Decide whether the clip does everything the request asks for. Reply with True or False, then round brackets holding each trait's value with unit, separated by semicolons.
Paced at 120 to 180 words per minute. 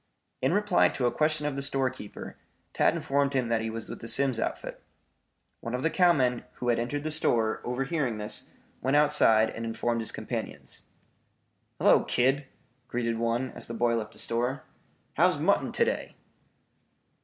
True (170 wpm)